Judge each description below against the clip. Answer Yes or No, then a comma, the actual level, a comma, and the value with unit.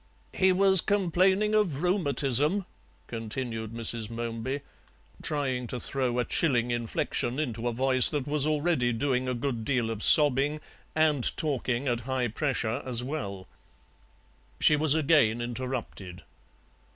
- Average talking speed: No, slow, 130 wpm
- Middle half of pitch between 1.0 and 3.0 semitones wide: No, average, 4.2 semitones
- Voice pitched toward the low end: Yes, low, 130 Hz